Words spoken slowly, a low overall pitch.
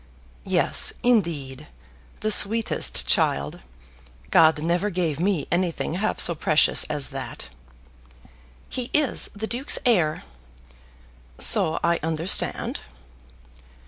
No: slow, 100 wpm; medium, 170 Hz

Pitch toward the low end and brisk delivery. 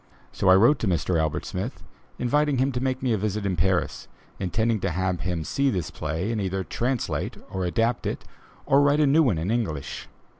Yes: low, 105 Hz; fast, 210 wpm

